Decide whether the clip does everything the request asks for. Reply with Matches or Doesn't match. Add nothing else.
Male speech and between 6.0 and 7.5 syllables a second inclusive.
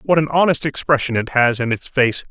Doesn't match